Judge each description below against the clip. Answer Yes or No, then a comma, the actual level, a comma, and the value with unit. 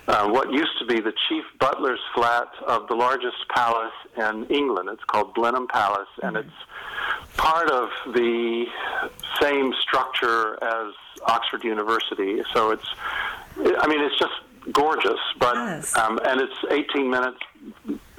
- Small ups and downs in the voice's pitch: No, average, 4.0 semitones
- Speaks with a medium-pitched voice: No, low, 120 Hz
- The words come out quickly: No, average, 140 wpm